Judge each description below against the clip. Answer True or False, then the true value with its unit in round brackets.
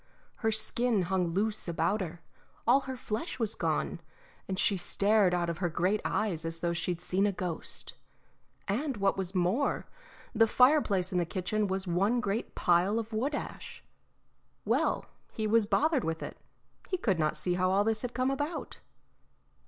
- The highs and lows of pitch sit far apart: False (4.2 semitones)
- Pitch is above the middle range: True (200 Hz)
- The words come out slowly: False (175 wpm)